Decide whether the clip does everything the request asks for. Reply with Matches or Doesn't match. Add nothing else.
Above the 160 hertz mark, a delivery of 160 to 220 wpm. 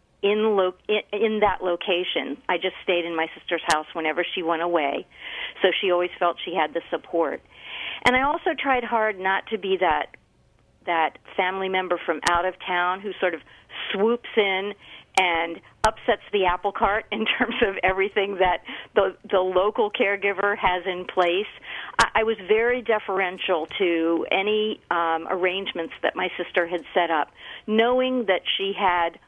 Matches